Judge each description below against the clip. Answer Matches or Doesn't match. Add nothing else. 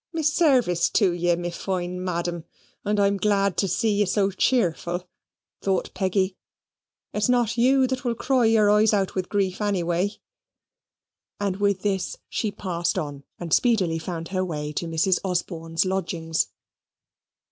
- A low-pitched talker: Doesn't match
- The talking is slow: Doesn't match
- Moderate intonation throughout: Matches